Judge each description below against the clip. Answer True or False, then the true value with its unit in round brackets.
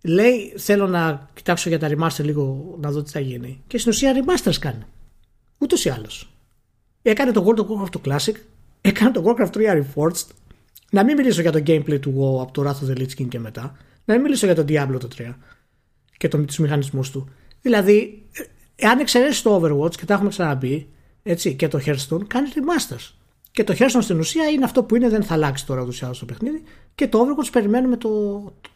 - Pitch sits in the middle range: True (175 Hz)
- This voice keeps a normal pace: False (210 wpm)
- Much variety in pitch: True (7.9 semitones)